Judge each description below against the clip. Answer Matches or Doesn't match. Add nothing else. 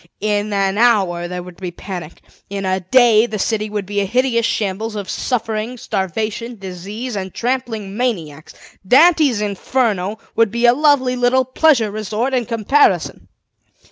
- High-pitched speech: Matches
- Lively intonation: Doesn't match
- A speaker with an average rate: Matches